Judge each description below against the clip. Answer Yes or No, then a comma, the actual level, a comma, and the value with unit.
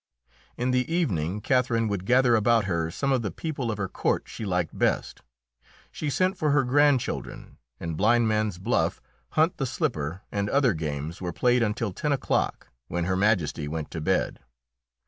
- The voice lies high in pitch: No, low, 110 Hz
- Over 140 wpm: Yes, average, 175 wpm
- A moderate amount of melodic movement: No, wide, 6.4 semitones